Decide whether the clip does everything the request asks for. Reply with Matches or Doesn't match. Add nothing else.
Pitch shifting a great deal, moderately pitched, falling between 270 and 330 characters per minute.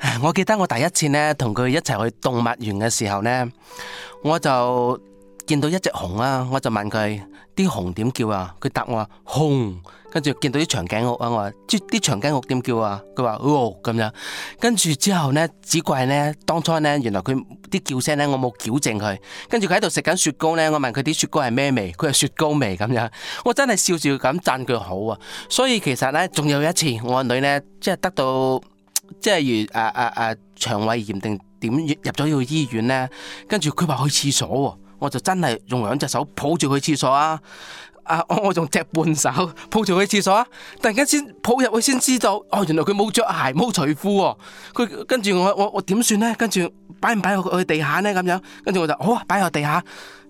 Matches